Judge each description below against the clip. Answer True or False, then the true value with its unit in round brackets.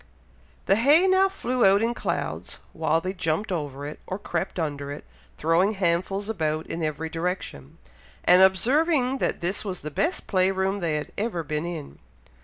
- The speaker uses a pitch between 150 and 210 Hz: True (185 Hz)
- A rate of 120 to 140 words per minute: False (175 wpm)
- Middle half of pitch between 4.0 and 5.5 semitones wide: True (5.0 semitones)